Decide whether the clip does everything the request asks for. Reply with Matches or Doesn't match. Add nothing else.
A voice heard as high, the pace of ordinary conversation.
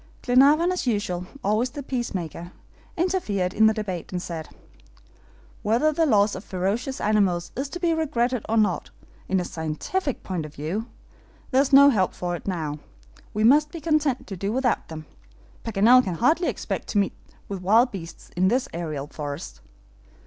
Matches